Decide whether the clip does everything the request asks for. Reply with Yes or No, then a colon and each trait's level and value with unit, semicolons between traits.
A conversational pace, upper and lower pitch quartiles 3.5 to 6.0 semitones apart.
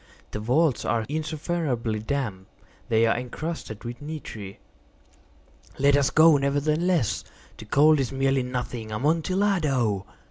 No: slow, 115 wpm; average, 5.3 semitones